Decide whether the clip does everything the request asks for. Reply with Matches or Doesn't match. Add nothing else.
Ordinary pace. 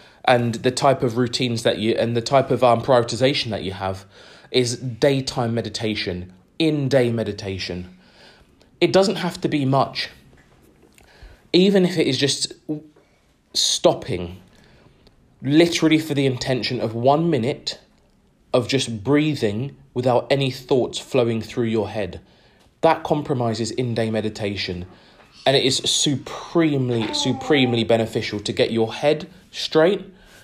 Doesn't match